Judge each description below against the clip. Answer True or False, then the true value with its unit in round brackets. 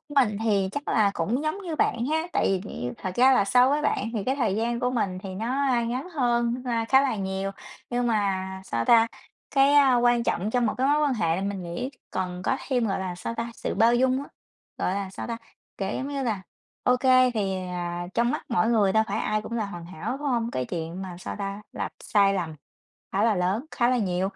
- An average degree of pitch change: True (4.7 semitones)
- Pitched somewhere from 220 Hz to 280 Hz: True (225 Hz)